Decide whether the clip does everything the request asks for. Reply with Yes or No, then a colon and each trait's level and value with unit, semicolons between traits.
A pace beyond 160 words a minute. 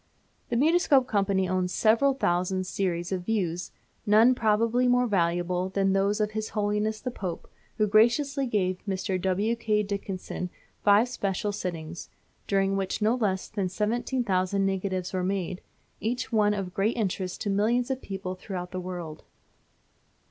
No: average, 150 wpm